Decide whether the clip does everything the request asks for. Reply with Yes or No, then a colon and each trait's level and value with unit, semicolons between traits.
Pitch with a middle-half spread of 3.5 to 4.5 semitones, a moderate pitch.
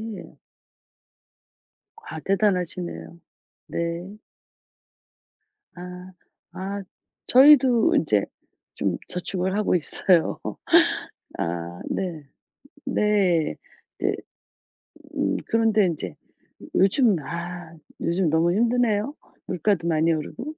Yes: average, 4.0 semitones; medium, 180 Hz